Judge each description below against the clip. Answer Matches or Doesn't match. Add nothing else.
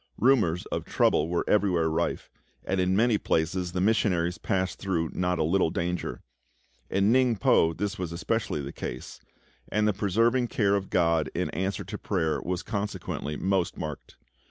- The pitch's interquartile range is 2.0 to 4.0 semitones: Matches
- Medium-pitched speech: Doesn't match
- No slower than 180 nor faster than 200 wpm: Doesn't match